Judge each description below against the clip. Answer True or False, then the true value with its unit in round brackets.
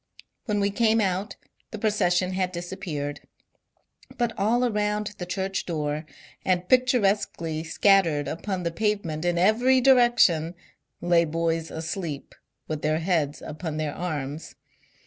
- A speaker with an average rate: False (130 wpm)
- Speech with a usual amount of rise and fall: True (4.5 semitones)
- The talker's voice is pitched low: False (180 Hz)